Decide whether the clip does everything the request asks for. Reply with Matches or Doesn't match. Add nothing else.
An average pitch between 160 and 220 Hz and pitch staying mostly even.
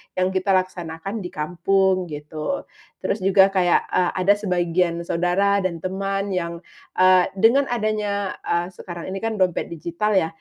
Matches